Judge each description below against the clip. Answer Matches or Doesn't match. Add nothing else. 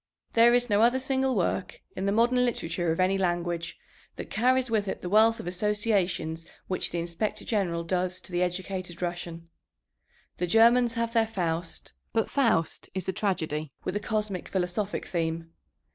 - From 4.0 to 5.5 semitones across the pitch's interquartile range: Matches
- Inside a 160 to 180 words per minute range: Matches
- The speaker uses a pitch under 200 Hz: Matches